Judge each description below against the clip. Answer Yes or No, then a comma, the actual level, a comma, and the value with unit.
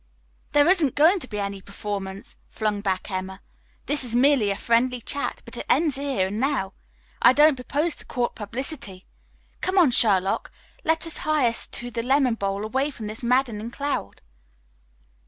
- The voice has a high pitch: Yes, high, 240 Hz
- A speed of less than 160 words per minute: No, average, 175 wpm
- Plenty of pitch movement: Yes, wide, 5.8 semitones